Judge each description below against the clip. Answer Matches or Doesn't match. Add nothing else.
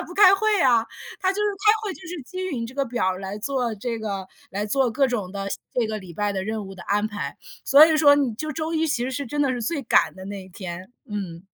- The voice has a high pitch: Matches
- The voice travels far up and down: Matches